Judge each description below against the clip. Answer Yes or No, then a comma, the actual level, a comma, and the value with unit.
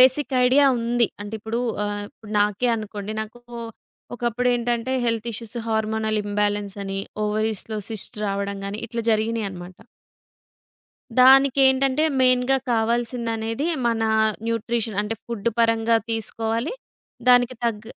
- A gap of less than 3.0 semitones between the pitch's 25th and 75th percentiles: Yes, narrow, 2.4 semitones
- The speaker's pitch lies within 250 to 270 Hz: No, high, 225 Hz